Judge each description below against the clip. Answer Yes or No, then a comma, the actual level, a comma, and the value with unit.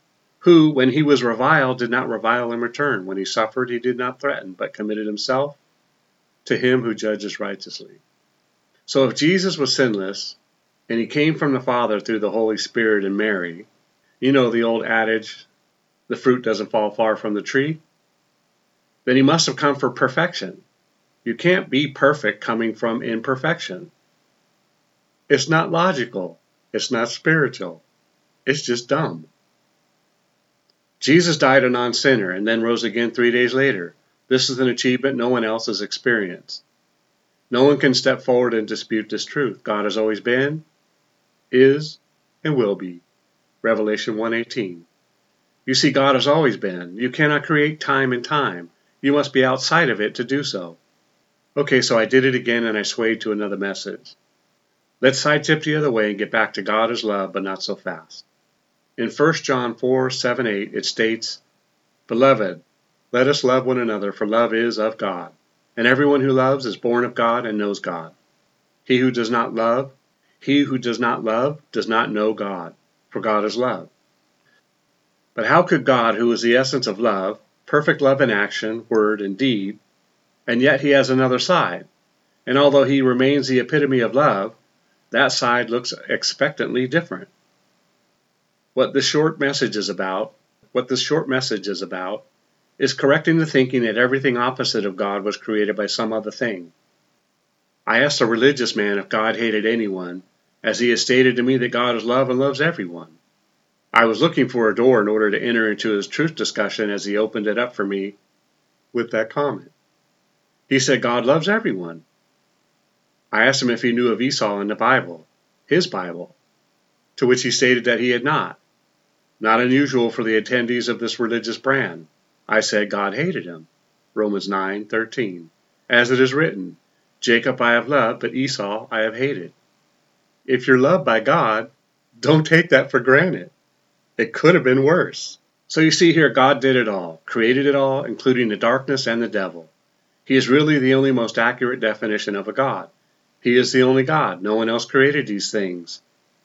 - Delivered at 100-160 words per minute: No, average, 175 wpm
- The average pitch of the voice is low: Yes, low, 120 Hz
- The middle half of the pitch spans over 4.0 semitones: No, average, 3.7 semitones